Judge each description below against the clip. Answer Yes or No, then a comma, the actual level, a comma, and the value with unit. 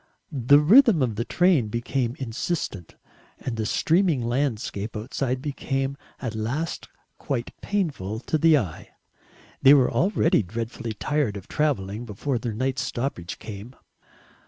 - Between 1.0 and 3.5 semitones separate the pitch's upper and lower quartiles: No, average, 4.8 semitones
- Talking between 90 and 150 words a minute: Yes, slow, 135 wpm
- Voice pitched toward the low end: Yes, low, 125 Hz